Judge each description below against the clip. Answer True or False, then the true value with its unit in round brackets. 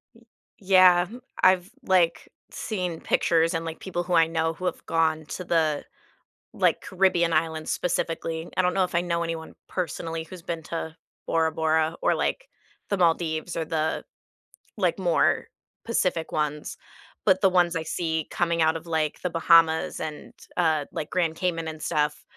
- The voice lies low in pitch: False (165 Hz)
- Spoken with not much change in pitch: True (1.9 semitones)